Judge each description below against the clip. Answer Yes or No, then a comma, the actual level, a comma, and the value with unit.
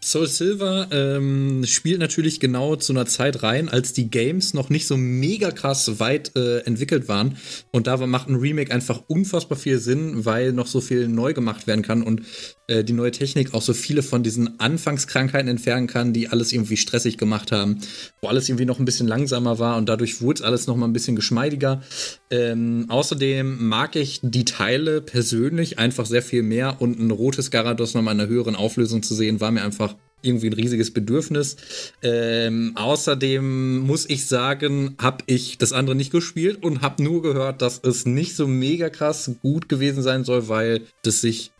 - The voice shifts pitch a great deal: No, average, 3.2 semitones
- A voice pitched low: Yes, low, 125 Hz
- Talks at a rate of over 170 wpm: Yes, fast, 190 wpm